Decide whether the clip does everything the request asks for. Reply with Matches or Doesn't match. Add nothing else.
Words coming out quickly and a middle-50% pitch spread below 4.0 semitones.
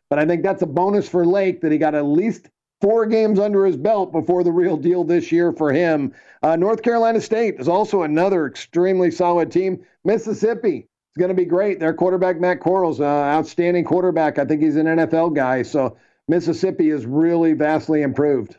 Doesn't match